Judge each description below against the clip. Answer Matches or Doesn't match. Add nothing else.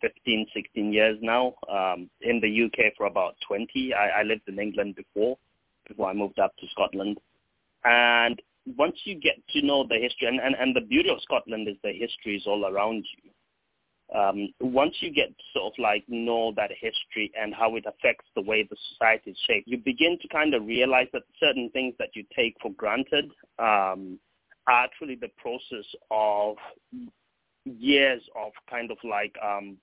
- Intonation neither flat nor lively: Matches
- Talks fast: Doesn't match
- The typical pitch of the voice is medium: Doesn't match